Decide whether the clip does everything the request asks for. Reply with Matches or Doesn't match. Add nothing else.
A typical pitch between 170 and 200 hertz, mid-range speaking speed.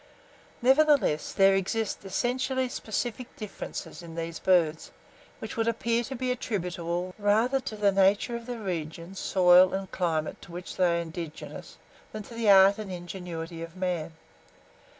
Matches